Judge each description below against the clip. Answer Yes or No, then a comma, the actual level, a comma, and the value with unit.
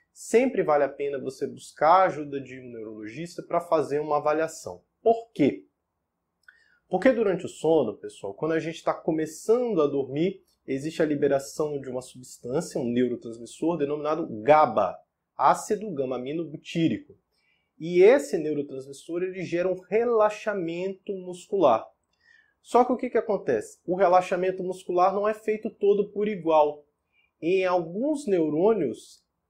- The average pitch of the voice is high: No, medium, 170 Hz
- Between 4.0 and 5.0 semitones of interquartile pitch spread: No, wide, 5.5 semitones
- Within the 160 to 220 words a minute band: No, average, 135 wpm